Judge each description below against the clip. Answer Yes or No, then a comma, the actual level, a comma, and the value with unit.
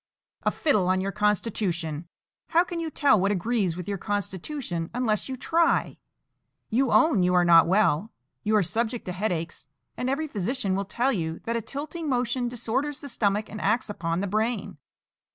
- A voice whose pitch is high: Yes, high, 215 Hz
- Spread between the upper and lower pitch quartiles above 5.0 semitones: Yes, wide, 5.4 semitones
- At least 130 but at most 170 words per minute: No, average, 180 wpm